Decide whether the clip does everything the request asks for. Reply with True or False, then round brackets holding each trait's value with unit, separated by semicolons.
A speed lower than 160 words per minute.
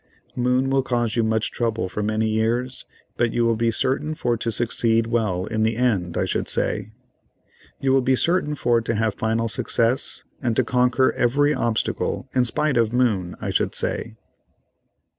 False (180 wpm)